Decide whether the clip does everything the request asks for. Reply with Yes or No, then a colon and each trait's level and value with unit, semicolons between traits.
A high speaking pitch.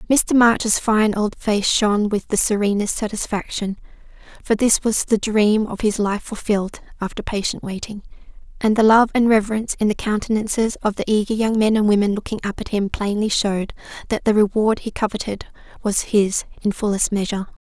Yes: high, 210 Hz